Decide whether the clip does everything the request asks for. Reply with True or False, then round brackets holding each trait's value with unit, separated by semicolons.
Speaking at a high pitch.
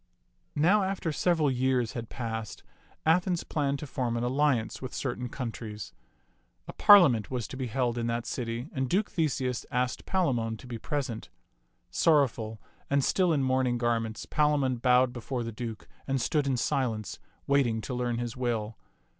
False (125 Hz)